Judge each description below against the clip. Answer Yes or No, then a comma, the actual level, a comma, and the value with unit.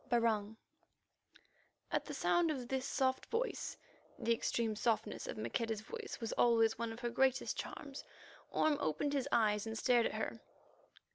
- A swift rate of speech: No, average, 155 wpm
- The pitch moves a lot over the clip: No, average, 3.2 semitones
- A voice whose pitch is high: Yes, high, 235 Hz